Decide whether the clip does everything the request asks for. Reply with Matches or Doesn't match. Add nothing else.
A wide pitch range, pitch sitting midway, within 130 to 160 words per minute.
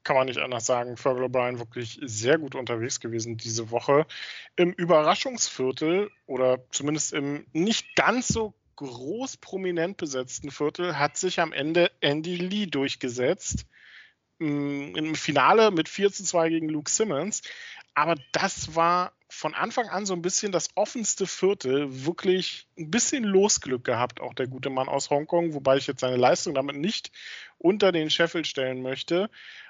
Matches